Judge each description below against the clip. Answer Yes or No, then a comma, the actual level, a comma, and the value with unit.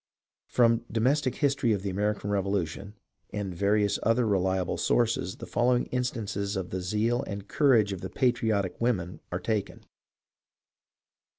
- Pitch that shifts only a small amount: No, average, 3.5 semitones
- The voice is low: Yes, low, 105 Hz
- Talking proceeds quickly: No, average, 150 wpm